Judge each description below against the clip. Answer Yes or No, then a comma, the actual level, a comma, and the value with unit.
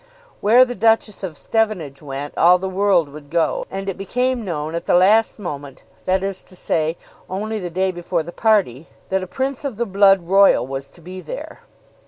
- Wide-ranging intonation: No, average, 4.1 semitones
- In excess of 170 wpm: Yes, average, 200 wpm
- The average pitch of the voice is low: No, high, 190 Hz